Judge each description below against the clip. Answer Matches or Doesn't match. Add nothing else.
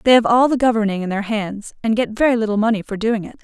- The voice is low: Doesn't match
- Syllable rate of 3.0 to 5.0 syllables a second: Doesn't match